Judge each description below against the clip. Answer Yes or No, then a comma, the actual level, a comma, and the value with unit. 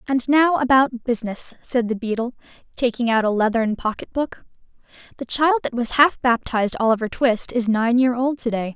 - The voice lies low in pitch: No, high, 240 Hz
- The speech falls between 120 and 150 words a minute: No, average, 185 wpm